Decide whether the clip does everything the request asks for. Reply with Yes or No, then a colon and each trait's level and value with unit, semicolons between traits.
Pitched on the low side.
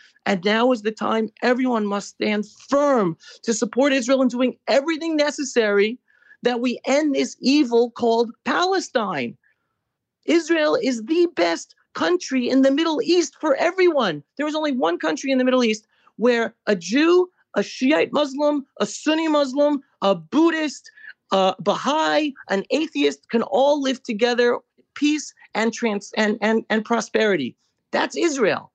No: very high, 255 Hz